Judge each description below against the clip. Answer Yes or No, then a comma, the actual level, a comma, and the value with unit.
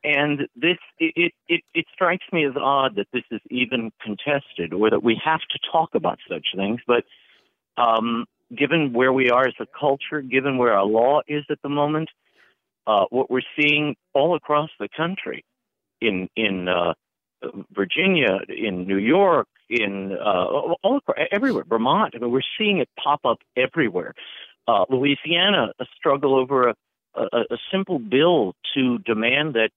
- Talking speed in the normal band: Yes, average, 165 wpm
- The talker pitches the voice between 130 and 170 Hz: Yes, low, 135 Hz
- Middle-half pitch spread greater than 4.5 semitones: Yes, average, 4.9 semitones